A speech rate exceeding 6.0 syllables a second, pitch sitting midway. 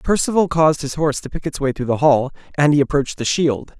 Yes: 6.4 syllables/s; medium, 145 Hz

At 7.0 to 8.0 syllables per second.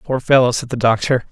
No: 5.9 syllables/s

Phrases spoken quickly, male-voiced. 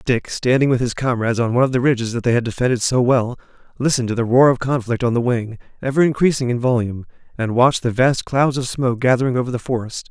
Yes: fast, 235 wpm; male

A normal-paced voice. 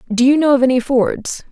No: fast, 235 wpm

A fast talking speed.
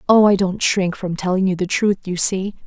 Yes: fast, 245 wpm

